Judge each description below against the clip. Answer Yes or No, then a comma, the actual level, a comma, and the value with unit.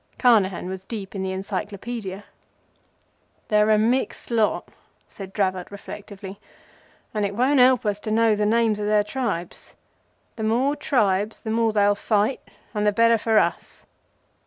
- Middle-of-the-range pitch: No, high, 210 Hz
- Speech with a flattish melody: Yes, narrow, 2.3 semitones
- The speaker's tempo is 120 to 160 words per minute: Yes, average, 155 wpm